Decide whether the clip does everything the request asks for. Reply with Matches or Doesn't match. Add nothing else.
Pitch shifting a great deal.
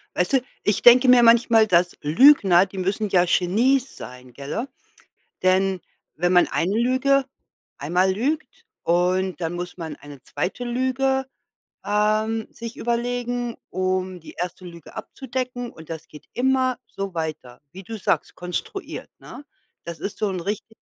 Matches